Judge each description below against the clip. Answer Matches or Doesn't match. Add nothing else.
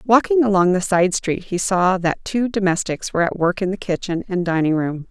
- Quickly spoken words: Matches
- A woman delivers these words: Matches